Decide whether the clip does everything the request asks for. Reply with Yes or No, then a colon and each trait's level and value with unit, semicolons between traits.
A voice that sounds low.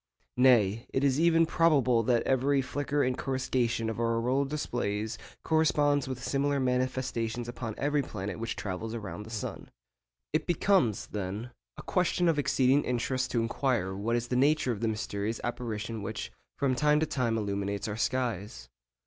Yes: low, 125 Hz